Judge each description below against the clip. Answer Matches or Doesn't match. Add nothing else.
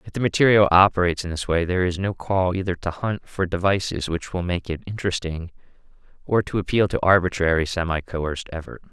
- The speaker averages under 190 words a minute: Doesn't match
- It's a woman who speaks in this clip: Doesn't match